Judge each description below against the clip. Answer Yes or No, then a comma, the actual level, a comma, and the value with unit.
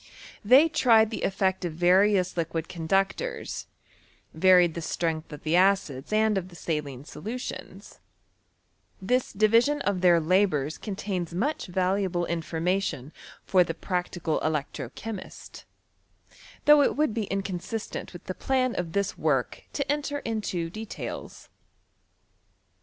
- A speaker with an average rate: No, slow, 125 wpm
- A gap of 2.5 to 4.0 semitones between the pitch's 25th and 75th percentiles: No, average, 4.5 semitones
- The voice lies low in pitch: No, medium, 185 Hz